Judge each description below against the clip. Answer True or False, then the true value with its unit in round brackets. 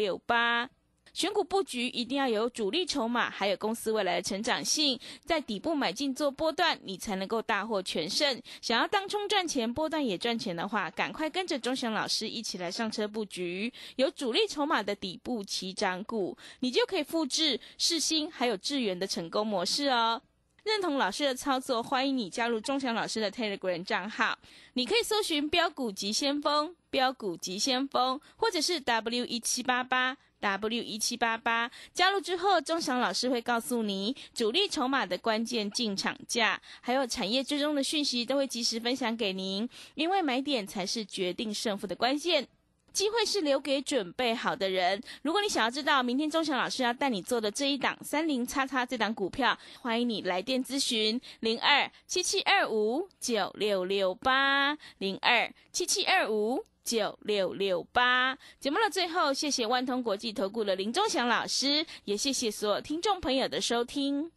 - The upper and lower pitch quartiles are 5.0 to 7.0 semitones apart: True (5.3 semitones)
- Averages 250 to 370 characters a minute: True (280 characters per minute)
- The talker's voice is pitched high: True (250 Hz)